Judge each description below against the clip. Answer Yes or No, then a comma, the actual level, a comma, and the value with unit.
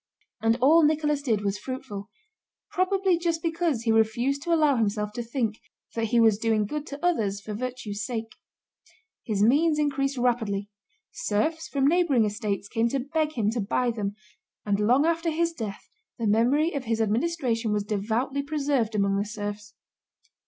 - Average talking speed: Yes, average, 165 wpm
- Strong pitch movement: Yes, wide, 5.9 semitones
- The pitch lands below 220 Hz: No, high, 240 Hz